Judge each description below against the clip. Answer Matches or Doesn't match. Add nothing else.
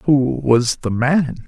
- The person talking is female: Doesn't match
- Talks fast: Doesn't match